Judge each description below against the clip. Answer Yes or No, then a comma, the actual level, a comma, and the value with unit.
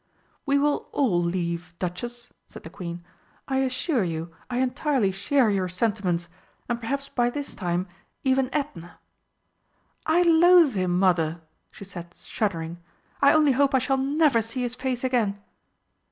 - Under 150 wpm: No, average, 155 wpm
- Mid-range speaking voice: No, high, 235 Hz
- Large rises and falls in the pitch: Yes, wide, 7.2 semitones